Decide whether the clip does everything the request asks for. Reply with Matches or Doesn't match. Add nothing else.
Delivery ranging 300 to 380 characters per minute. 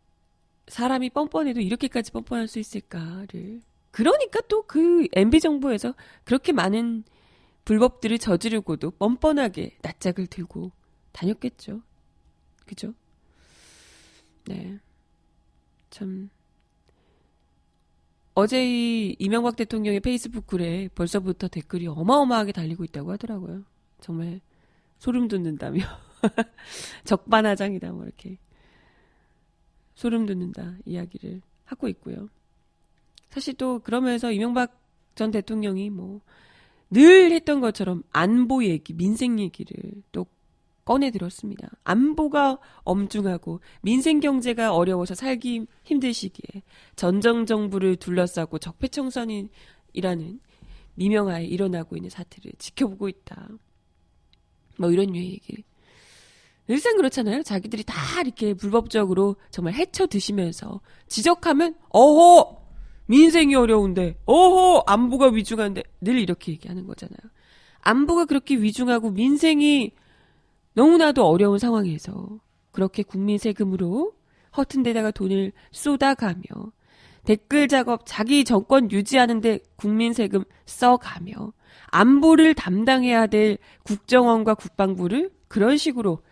Doesn't match